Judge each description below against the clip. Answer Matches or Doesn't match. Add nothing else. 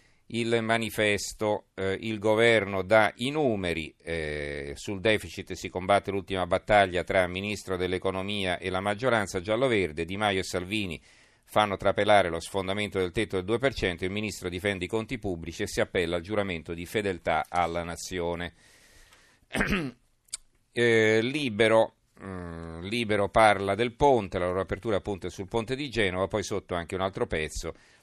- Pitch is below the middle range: Matches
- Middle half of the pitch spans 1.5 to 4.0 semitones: Matches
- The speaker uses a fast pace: Doesn't match